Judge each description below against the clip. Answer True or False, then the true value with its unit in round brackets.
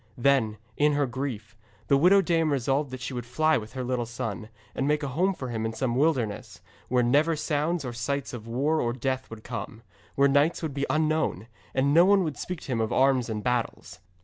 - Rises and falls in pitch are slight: False (4.1 semitones)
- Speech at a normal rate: False (220 wpm)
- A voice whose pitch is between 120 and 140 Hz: True (135 Hz)